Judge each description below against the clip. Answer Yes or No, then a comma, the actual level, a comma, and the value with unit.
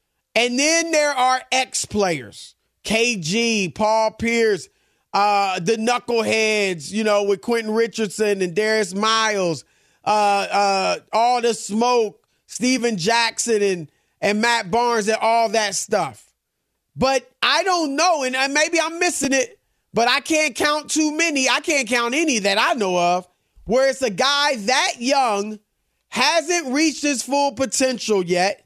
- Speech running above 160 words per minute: No, average, 145 wpm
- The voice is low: No, high, 230 Hz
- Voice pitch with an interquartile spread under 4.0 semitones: No, average, 4.6 semitones